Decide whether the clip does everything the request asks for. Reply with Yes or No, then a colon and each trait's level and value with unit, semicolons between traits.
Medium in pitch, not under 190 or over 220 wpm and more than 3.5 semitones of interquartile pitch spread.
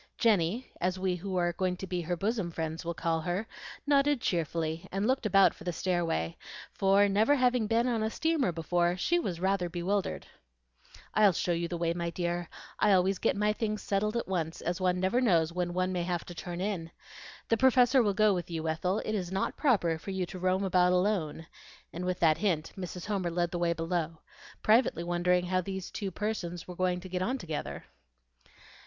No: medium, 180 Hz; fast, 205 wpm; average, 3.1 semitones